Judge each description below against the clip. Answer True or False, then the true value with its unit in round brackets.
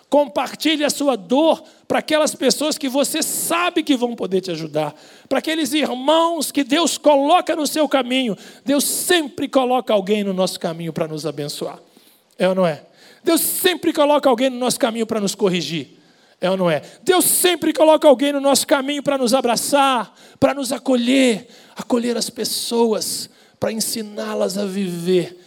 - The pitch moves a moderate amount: False (5.9 semitones)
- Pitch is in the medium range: False (260 Hz)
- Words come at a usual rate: True (170 wpm)